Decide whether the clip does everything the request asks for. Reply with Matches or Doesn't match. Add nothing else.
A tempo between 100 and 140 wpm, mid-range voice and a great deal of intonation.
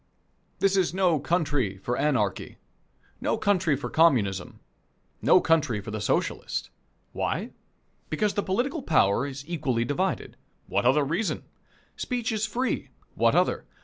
Matches